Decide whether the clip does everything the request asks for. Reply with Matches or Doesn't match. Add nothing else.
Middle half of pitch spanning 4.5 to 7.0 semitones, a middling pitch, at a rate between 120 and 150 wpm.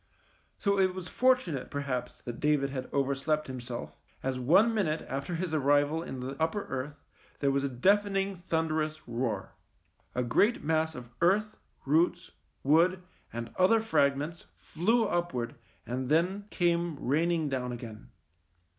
Matches